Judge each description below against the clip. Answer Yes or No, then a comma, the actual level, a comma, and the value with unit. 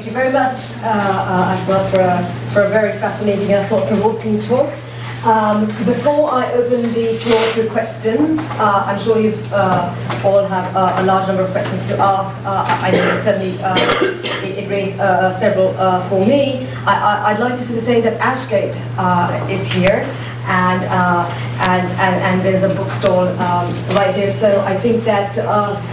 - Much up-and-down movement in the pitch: No, average, 3.4 semitones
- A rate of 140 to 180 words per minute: No, average, 195 wpm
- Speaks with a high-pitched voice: Yes, high, 200 Hz